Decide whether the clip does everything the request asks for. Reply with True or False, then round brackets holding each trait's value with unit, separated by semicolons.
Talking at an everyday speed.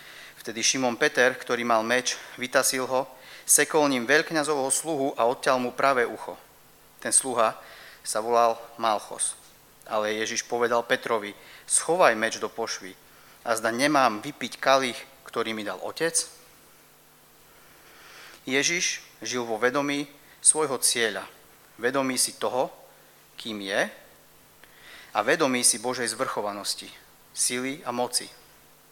True (120 wpm)